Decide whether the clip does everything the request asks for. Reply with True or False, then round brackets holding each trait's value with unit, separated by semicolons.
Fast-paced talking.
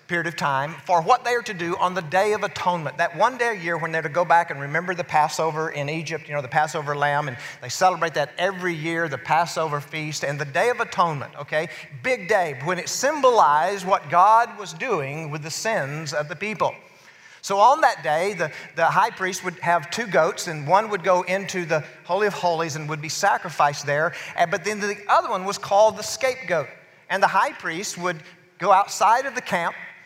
True (220 wpm)